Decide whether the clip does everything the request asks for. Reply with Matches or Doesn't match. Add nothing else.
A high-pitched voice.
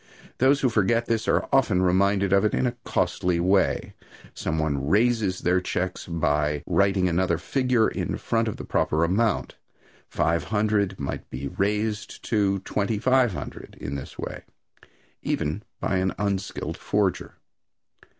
Doesn't match